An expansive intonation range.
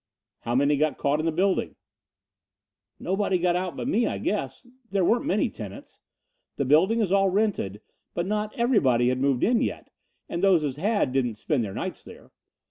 Yes: wide, 6.6 semitones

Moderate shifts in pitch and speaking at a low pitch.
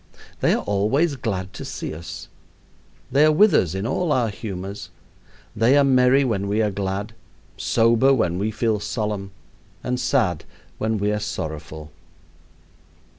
Yes: average, 4.5 semitones; low, 105 Hz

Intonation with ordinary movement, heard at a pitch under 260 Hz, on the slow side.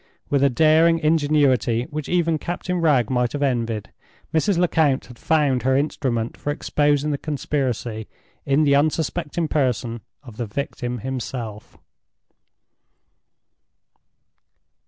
Yes: average, 4.0 semitones; medium, 140 Hz; slow, 115 wpm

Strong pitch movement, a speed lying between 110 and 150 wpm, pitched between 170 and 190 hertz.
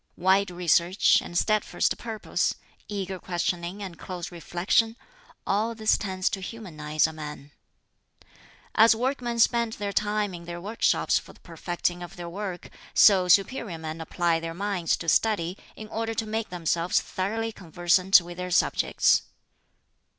No: average, 3.7 semitones; average, 145 wpm; medium, 185 Hz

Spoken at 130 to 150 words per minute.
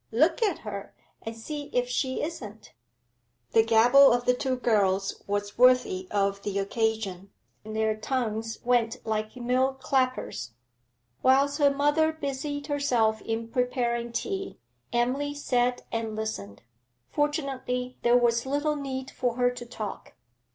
Yes: slow, 135 wpm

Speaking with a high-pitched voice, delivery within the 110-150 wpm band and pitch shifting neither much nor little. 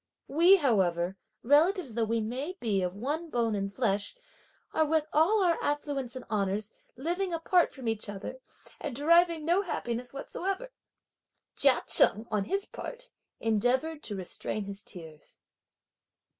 No: very high, 255 Hz; average, 145 wpm; wide, 7.6 semitones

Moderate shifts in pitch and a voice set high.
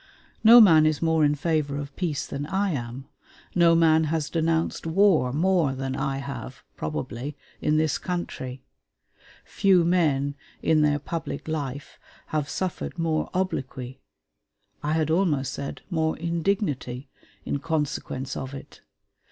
No: average, 3.3 semitones; medium, 155 Hz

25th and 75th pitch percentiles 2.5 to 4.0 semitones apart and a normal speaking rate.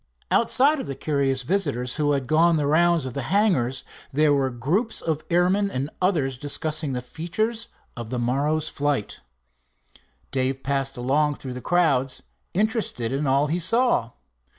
No: average, 4.7 semitones; average, 155 wpm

